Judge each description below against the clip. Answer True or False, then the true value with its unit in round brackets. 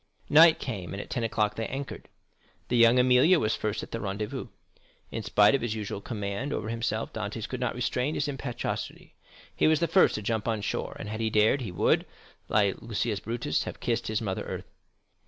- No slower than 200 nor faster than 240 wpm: True (205 wpm)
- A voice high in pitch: False (115 Hz)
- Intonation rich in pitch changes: False (3.1 semitones)